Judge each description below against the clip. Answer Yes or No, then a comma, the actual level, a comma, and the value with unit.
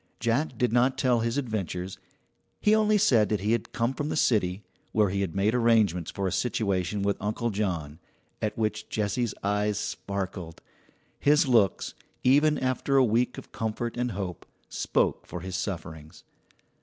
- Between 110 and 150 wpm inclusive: No, average, 165 wpm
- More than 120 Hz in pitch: No, low, 110 Hz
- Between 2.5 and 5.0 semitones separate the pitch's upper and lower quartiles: Yes, average, 4.1 semitones